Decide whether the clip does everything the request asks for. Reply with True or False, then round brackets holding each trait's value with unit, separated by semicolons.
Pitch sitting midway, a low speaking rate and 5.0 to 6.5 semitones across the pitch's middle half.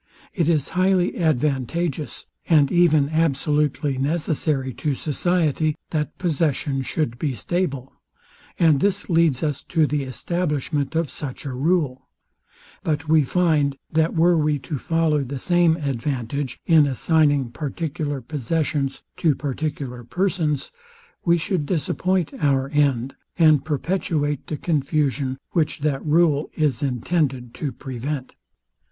False (150 Hz; 125 wpm; 3.2 semitones)